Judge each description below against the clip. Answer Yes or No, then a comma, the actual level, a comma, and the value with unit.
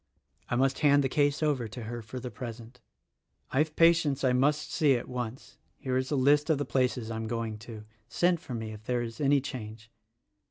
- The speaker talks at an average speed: No, fast, 215 wpm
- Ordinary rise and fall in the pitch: Yes, average, 3.7 semitones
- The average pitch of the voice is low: Yes, low, 130 Hz